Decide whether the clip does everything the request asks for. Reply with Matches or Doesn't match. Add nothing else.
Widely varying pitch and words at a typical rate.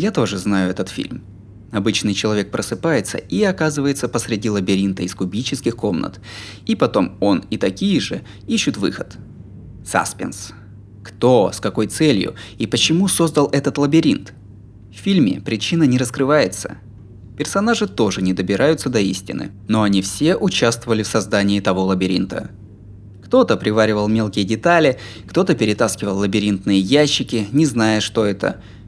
Matches